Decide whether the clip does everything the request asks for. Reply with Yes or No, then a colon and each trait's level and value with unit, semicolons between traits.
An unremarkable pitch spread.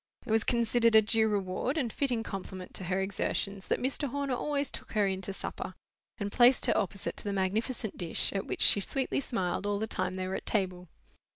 Yes: average, 4.0 semitones